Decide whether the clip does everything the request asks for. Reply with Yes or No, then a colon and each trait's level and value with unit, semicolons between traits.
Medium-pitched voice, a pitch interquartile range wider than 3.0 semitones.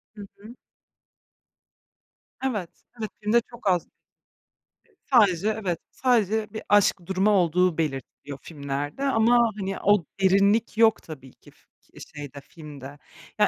No: high, 195 Hz; wide, 5.5 semitones